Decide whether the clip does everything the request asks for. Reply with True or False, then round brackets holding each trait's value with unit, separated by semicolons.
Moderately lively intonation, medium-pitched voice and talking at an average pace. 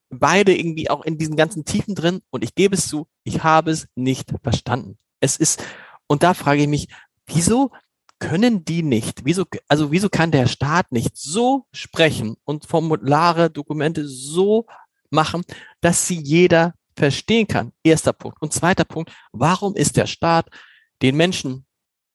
True (3.4 semitones; 160 Hz; 160 wpm)